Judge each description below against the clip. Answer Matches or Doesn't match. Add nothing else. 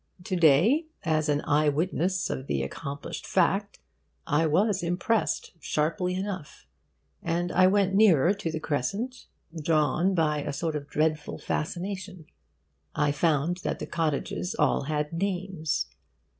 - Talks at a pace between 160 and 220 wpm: Doesn't match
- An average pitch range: Matches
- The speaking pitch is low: Doesn't match